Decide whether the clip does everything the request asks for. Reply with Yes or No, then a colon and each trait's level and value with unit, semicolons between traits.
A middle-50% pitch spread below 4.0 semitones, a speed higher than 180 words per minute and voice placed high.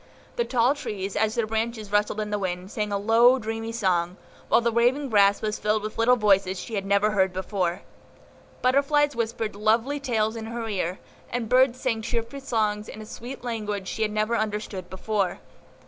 Yes: narrow, 2.5 semitones; average, 190 wpm; high, 220 Hz